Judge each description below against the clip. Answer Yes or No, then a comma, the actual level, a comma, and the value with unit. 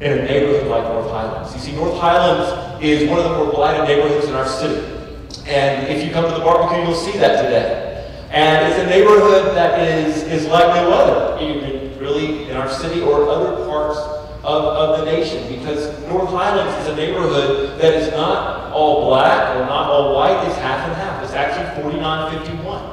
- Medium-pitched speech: Yes, medium, 150 Hz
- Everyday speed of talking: Yes, average, 195 wpm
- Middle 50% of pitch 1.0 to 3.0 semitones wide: Yes, narrow, 2.6 semitones